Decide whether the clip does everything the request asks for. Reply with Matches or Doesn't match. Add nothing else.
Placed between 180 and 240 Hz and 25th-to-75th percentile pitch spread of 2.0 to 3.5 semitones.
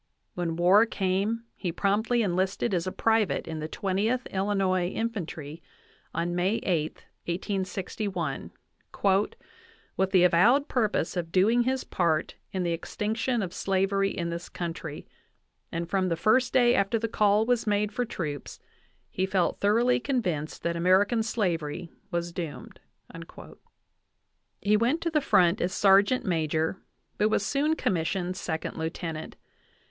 Doesn't match